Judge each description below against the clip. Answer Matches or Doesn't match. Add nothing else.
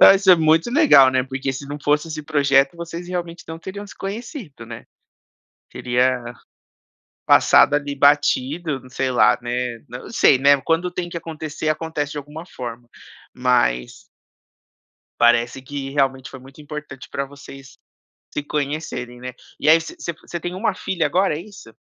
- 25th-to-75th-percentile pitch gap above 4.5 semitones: Doesn't match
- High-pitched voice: Doesn't match